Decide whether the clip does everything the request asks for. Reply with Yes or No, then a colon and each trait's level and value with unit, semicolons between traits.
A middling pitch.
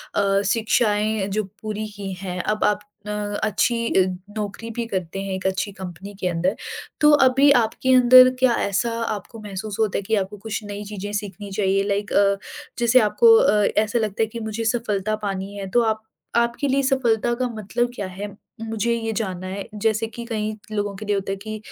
No: high, 210 Hz